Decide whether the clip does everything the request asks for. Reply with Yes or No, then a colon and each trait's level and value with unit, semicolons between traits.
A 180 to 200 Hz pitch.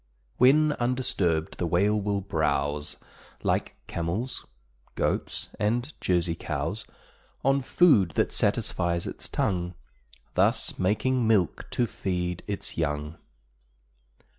No: very low, 95 Hz